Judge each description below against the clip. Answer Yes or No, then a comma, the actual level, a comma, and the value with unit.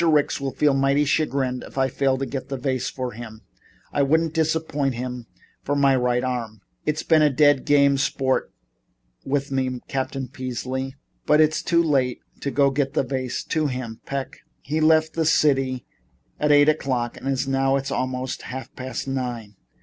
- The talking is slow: No, average, 175 wpm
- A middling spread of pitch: No, narrow, 2.1 semitones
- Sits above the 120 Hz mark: Yes, low, 135 Hz